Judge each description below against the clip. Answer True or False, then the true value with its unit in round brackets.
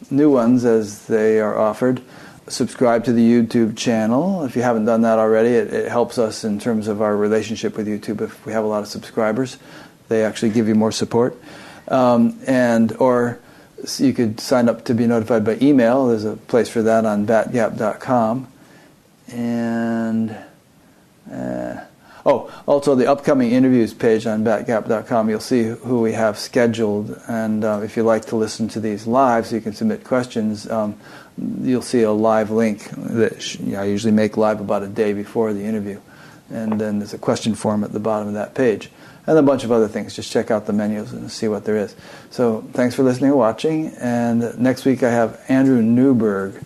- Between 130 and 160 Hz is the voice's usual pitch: False (115 Hz)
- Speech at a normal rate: True (195 wpm)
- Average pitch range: False (2.2 semitones)